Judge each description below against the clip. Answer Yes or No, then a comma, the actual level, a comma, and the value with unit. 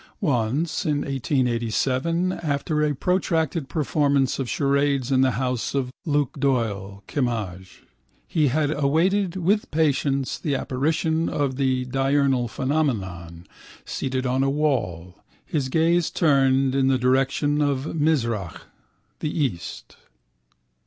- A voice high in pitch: No, low, 135 Hz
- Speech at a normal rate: No, slow, 120 wpm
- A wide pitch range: No, average, 3.0 semitones